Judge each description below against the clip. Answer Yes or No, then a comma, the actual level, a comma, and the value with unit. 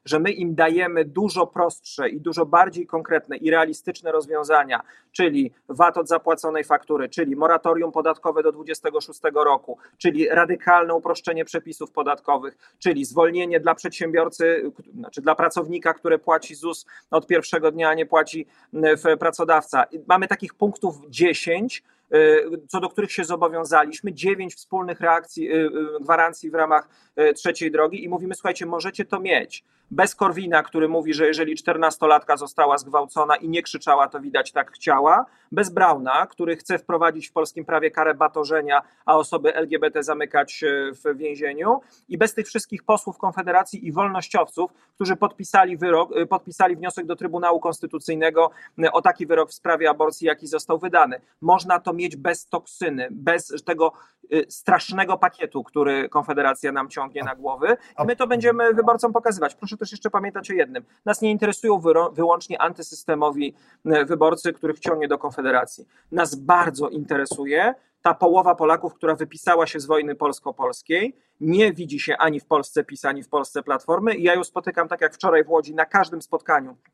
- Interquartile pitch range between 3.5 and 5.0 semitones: No, average, 2.9 semitones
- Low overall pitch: No, medium, 165 Hz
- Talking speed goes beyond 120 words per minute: Yes, average, 155 wpm